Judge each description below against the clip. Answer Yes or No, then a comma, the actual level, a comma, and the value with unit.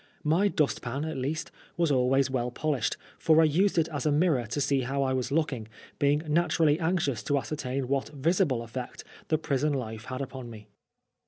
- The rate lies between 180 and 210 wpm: Yes, average, 190 wpm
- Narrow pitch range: No, average, 3.5 semitones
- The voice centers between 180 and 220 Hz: No, medium, 140 Hz